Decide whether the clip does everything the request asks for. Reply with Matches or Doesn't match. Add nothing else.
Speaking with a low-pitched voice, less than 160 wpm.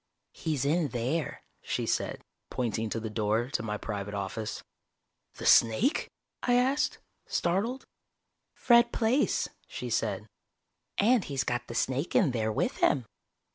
Matches